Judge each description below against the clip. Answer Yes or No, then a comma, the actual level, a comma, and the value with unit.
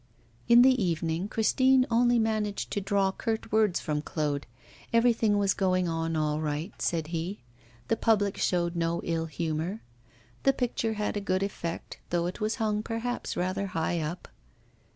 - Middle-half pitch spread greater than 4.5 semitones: Yes, average, 4.9 semitones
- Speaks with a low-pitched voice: No, high, 190 Hz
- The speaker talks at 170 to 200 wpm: No, average, 160 wpm